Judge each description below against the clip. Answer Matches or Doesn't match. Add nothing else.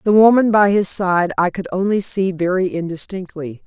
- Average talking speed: Matches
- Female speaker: Matches